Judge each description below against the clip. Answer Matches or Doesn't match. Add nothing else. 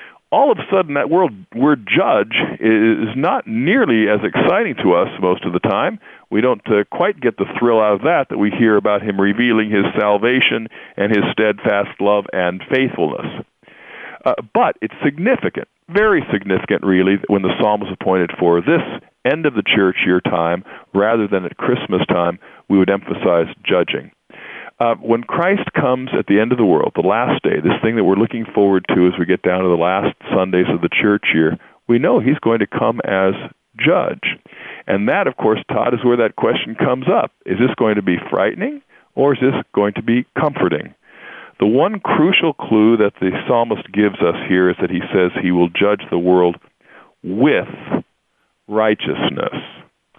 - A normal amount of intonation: Matches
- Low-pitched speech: Matches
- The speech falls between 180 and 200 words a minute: Matches